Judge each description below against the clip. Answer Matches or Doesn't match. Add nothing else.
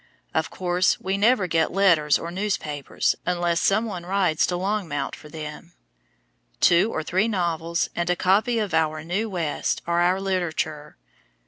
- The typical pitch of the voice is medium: Matches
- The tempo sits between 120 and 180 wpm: Matches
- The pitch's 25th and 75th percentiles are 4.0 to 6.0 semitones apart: Doesn't match